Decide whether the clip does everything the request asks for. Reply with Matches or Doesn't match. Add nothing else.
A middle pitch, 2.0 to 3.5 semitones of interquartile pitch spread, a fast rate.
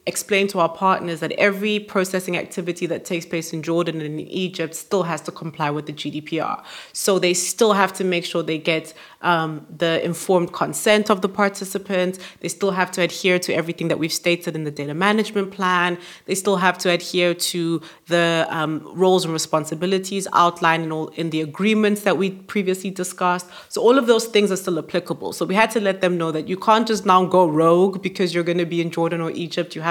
Matches